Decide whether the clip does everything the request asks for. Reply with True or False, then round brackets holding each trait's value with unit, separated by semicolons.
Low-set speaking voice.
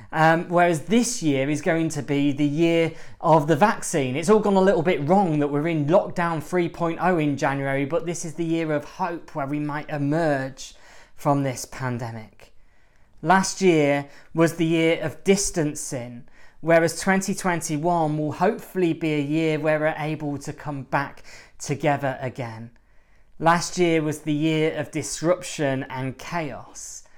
False (155 Hz)